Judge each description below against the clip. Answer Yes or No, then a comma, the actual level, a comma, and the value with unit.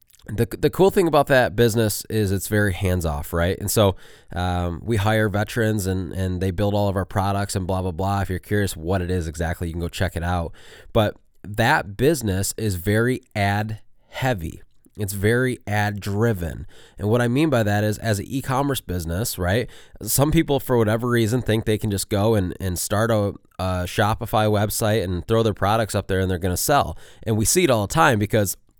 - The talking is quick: Yes, fast, 215 wpm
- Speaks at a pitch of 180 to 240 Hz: No, low, 105 Hz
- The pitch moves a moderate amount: Yes, average, 3.2 semitones